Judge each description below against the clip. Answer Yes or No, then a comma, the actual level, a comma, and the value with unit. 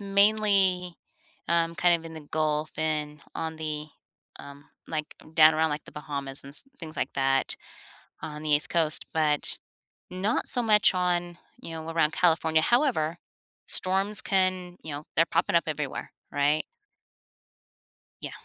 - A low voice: No, medium, 160 Hz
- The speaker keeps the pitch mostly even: No, average, 3.0 semitones